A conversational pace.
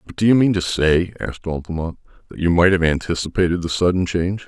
No: fast, 215 wpm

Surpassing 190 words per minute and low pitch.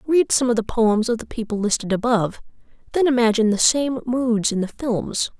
No: average, 200 wpm; high, 230 Hz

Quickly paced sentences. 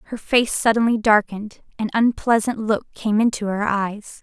No: average, 155 wpm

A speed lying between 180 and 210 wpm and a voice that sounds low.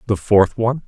Yes: fast, 205 wpm; low, 110 Hz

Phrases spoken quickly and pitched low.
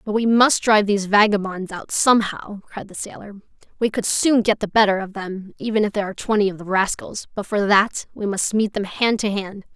No: fast, 230 wpm; high, 205 Hz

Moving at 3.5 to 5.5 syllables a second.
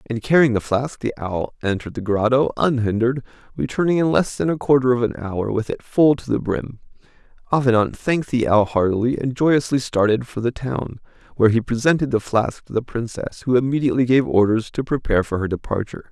No: 5.9 syllables/s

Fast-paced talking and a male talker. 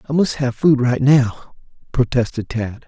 No: average, 165 wpm; male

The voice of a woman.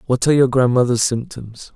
No: male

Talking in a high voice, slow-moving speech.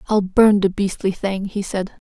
No: high, 195 Hz; average, 200 wpm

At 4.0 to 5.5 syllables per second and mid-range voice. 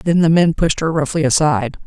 No: 6.0 syllables/s; medium, 155 Hz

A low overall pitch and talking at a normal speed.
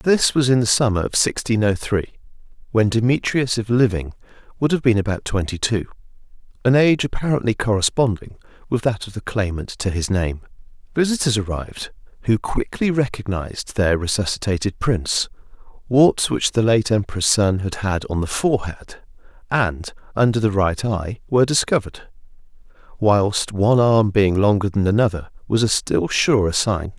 Yes: low, 110 Hz; average, 150 wpm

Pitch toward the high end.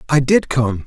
No: low, 135 Hz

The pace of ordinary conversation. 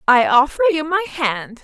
Yes: average, 185 wpm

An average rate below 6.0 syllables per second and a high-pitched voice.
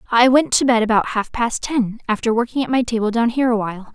No: 6.3 syllables/s; high, 230 Hz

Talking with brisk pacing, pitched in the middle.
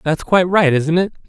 Yes: fast, 235 wpm; medium, 170 Hz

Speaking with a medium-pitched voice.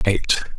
No: very low, 95 Hz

